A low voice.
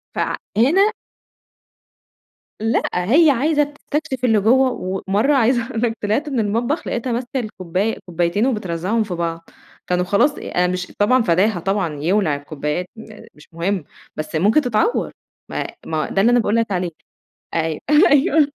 No: high, 215 Hz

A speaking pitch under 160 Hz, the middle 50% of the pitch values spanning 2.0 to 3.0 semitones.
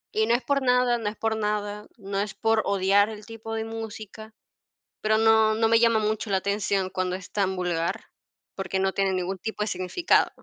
No: high, 210 Hz; narrow, 2.4 semitones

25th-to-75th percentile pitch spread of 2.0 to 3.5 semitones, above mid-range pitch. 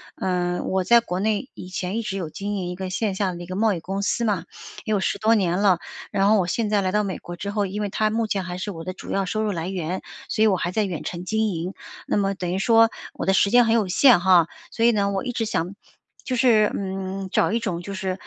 Yes: average, 2.7 semitones; high, 195 Hz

